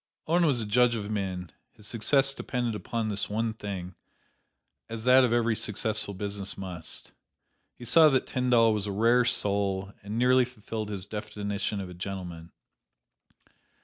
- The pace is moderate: Yes, average, 155 wpm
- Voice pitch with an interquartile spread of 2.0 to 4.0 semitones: Yes, average, 3.2 semitones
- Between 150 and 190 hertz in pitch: No, low, 105 Hz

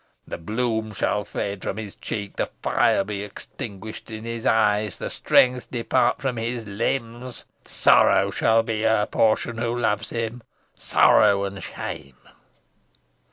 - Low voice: Yes, low, 110 Hz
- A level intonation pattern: Yes, narrow, 2.2 semitones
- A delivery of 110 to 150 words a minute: Yes, average, 140 wpm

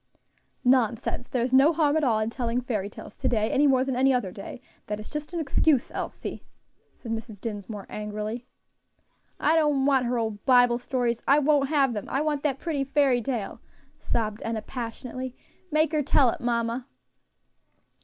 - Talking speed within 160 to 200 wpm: Yes, average, 175 wpm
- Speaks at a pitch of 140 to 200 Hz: No, very high, 250 Hz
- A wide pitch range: No, average, 3.5 semitones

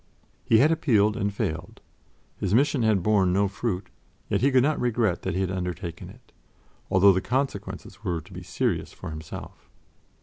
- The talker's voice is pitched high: No, low, 100 Hz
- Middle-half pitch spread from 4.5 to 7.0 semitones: Yes, average, 5.0 semitones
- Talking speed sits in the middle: Yes, average, 175 wpm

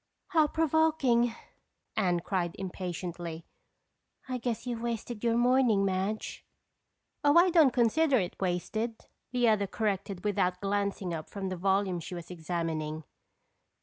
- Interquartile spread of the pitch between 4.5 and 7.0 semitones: Yes, average, 5.1 semitones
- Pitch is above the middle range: Yes, high, 200 Hz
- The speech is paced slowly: Yes, slow, 130 wpm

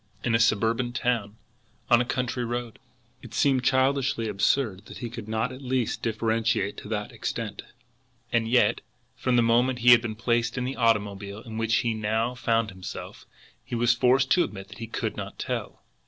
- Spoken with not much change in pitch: Yes, narrow, 1.9 semitones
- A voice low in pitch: Yes, low, 115 Hz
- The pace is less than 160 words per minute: No, average, 185 wpm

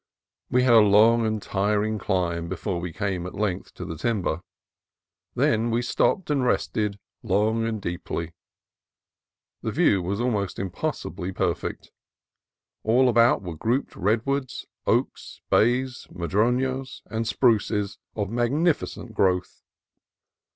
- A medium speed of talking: No, slow, 125 wpm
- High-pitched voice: No, low, 110 Hz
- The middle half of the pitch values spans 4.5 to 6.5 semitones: No, average, 4.0 semitones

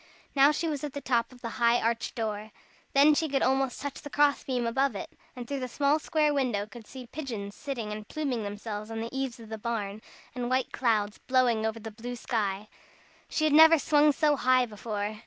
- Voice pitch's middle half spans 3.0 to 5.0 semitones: Yes, average, 4.1 semitones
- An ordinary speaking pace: No, fast, 215 wpm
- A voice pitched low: No, high, 245 Hz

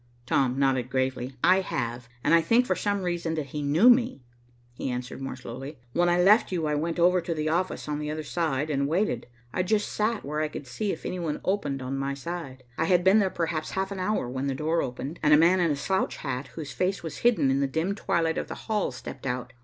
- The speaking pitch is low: No, medium, 155 Hz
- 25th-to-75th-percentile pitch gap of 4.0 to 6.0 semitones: Yes, average, 5.0 semitones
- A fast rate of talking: Yes, fast, 245 wpm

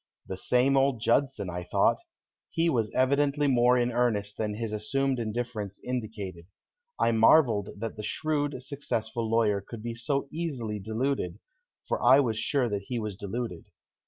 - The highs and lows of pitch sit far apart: No, average, 4.1 semitones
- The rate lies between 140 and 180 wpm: Yes, average, 160 wpm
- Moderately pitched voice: No, low, 115 Hz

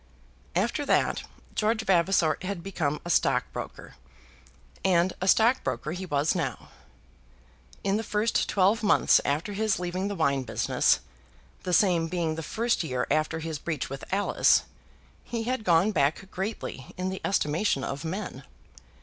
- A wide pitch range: No, average, 4.5 semitones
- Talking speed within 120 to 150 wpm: Yes, average, 145 wpm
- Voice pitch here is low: No, medium, 180 Hz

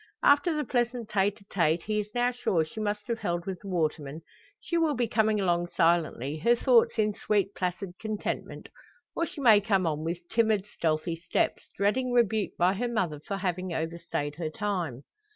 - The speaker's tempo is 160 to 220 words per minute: Yes, average, 190 wpm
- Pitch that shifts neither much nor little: Yes, average, 4.7 semitones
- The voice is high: Yes, high, 195 Hz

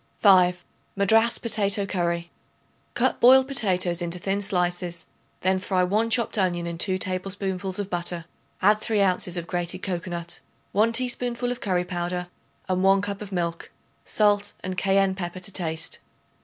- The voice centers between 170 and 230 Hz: Yes, medium, 185 Hz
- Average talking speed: Yes, average, 155 wpm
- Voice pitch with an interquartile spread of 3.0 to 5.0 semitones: No, narrow, 2.5 semitones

